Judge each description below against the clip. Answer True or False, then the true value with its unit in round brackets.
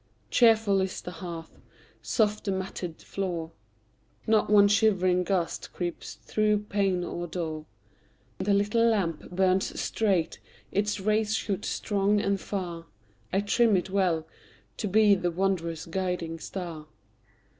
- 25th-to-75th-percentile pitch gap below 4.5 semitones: True (3.0 semitones)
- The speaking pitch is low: False (190 Hz)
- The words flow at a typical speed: False (130 wpm)